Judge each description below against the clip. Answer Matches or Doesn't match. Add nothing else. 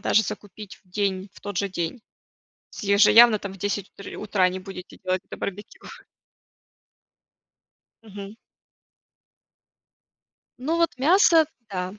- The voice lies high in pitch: Matches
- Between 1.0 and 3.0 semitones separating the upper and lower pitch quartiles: Matches